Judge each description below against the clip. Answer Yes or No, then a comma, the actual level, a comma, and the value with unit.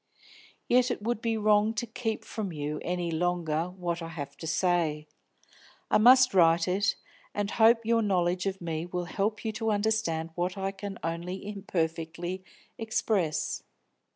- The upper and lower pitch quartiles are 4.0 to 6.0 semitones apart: Yes, average, 4.3 semitones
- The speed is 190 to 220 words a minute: No, average, 155 wpm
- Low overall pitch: No, medium, 185 Hz